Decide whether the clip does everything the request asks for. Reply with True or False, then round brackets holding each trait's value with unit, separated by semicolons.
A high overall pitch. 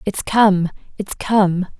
True (195 Hz)